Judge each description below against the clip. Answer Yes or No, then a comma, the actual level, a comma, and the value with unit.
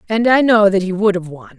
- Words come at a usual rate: No, fast, 300 wpm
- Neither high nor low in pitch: No, high, 200 Hz